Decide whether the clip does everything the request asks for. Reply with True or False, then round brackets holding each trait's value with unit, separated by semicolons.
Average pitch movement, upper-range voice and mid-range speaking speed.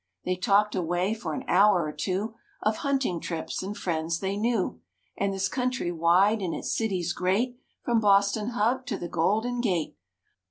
True (4.0 semitones; 200 Hz; 170 wpm)